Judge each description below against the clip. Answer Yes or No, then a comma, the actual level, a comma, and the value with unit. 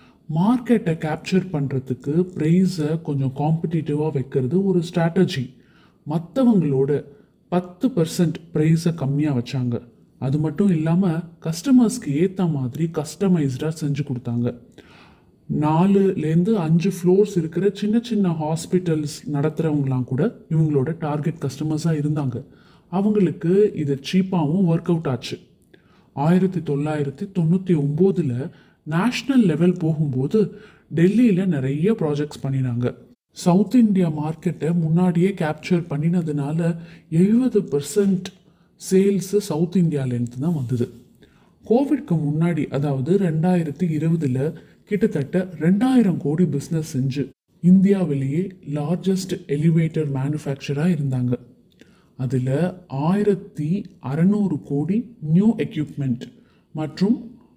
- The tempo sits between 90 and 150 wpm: No, average, 80 wpm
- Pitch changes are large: No, average, 4.2 semitones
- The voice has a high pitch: No, medium, 165 Hz